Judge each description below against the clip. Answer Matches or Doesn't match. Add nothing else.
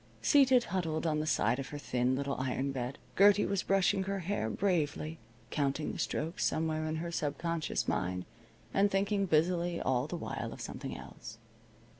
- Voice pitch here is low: Doesn't match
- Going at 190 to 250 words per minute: Doesn't match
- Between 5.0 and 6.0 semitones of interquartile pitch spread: Matches